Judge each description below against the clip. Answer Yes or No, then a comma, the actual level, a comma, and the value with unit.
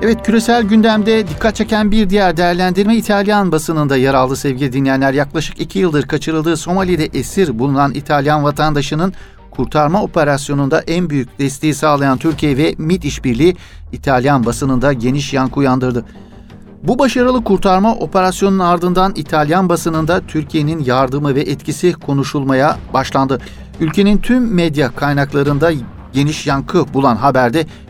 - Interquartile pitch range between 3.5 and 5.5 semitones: Yes, average, 5.0 semitones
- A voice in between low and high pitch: Yes, medium, 155 Hz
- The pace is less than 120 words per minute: No, average, 125 wpm